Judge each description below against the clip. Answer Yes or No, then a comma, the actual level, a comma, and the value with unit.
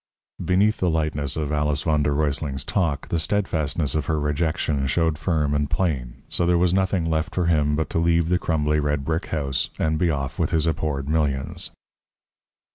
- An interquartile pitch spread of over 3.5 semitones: No, narrow, 2.4 semitones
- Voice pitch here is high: No, very low, 80 Hz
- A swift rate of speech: No, average, 190 wpm